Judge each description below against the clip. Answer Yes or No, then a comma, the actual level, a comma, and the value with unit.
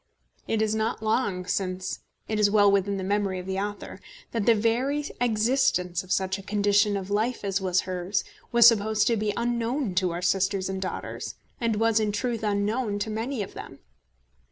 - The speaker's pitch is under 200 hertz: No, high, 205 Hz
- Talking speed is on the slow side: No, average, 190 wpm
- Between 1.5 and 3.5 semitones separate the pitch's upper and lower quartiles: Yes, average, 2.8 semitones